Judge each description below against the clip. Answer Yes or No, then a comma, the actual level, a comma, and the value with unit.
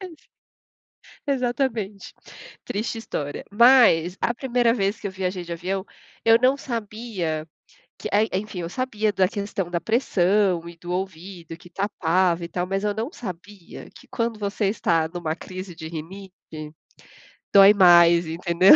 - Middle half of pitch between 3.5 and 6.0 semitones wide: Yes, average, 4.1 semitones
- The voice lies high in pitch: Yes, high, 195 Hz